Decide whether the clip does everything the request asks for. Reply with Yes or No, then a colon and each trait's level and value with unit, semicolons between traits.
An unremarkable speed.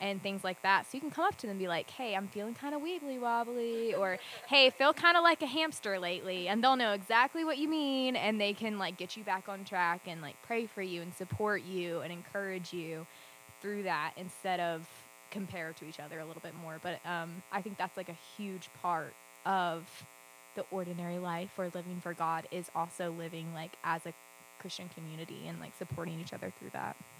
No: fast, 225 wpm